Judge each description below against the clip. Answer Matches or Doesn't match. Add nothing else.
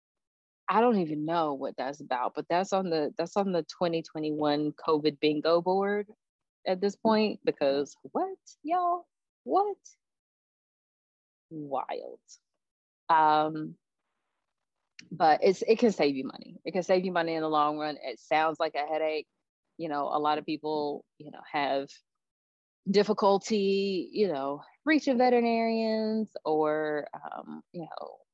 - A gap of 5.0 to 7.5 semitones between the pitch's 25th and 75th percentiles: Matches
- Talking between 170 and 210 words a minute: Doesn't match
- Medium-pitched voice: Matches